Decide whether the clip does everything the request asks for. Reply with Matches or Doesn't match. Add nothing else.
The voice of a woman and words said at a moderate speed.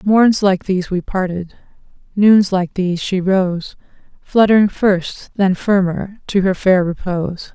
Matches